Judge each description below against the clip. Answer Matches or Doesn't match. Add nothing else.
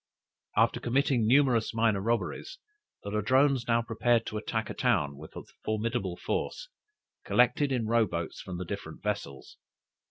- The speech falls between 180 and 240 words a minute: Doesn't match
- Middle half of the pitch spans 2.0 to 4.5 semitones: Matches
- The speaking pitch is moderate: Doesn't match